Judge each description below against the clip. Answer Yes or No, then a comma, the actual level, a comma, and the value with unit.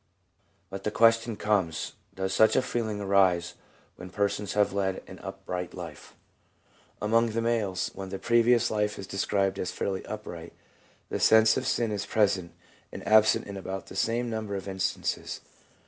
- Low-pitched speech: Yes, low, 100 Hz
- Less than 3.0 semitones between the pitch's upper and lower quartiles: Yes, narrow, 2.6 semitones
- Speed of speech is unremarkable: Yes, average, 165 wpm